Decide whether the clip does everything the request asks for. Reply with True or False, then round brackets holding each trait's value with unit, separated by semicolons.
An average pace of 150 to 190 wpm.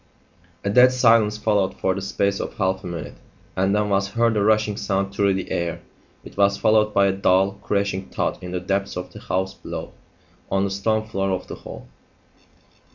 False (200 wpm)